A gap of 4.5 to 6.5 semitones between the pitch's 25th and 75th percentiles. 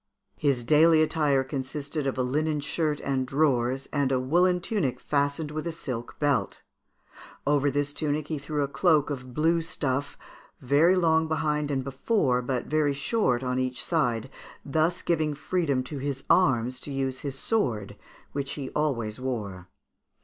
No: average, 3.1 semitones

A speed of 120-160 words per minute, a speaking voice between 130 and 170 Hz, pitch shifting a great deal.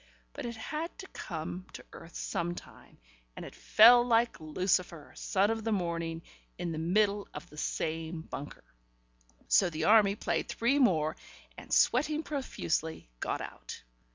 No: average, 150 wpm; medium, 185 Hz; wide, 5.8 semitones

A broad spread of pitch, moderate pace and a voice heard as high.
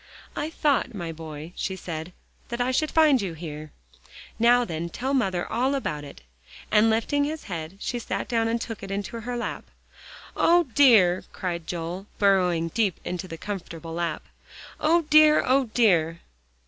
Yes: wide, 6.7 semitones; average, 165 wpm; high, 200 Hz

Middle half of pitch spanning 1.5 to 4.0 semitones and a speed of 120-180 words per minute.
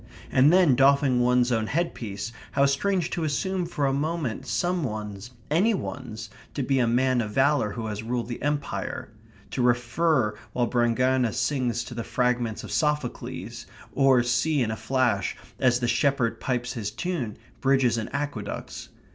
Yes: average, 3.4 semitones; average, 165 wpm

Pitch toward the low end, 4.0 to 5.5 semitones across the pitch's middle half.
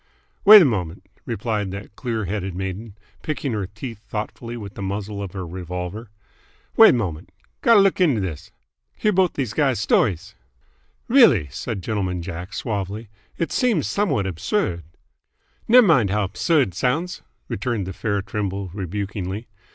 Yes: low, 105 Hz; average, 4.9 semitones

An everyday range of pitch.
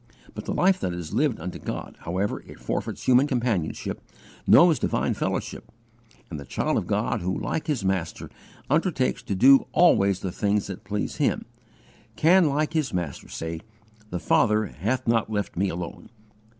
No: wide, 7.5 semitones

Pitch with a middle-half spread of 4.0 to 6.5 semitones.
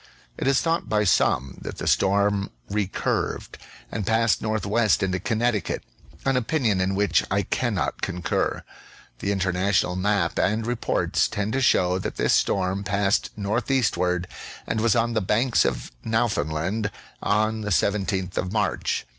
No: average, 3.0 semitones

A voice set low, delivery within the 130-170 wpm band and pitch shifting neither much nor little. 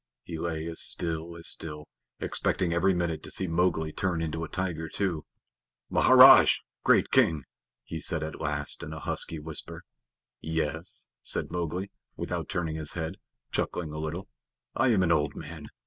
No: very low, 80 Hz; average, 165 wpm; narrow, 1.9 semitones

